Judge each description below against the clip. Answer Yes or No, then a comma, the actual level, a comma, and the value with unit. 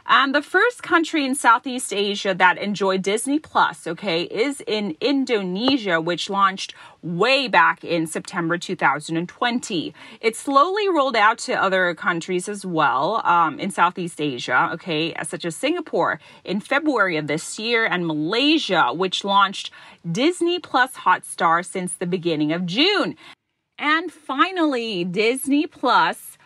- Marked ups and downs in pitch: Yes, wide, 7.7 semitones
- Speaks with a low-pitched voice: No, high, 205 Hz